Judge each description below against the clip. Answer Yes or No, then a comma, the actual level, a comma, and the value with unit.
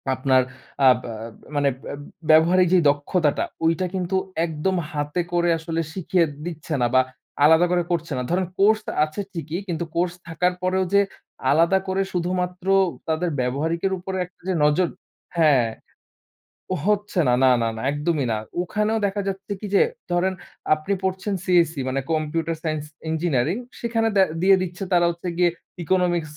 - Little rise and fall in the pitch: No, average, 3.2 semitones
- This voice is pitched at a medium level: Yes, medium, 175 Hz